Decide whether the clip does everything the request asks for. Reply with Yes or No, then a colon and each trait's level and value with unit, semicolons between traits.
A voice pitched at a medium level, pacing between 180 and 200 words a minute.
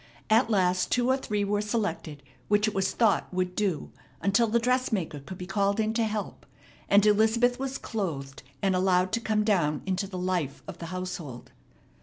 No: high, 200 Hz; average, 185 wpm